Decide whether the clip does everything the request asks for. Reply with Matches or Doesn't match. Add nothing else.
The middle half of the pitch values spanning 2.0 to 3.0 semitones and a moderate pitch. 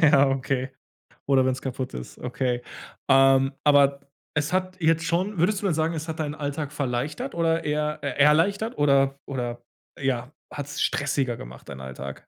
Doesn't match